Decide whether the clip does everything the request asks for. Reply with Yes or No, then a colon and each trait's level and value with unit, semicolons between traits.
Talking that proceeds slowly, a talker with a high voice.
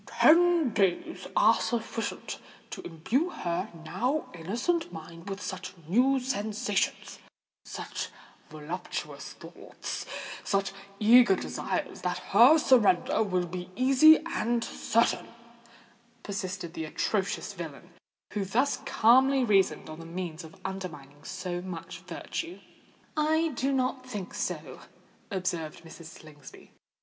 Yes: slow, 110 wpm; high, 195 Hz